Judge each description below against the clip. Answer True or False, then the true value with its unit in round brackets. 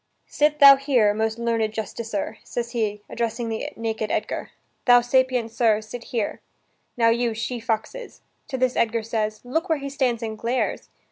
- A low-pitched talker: False (230 Hz)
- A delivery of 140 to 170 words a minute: True (165 wpm)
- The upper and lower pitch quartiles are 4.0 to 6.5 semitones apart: False (2.4 semitones)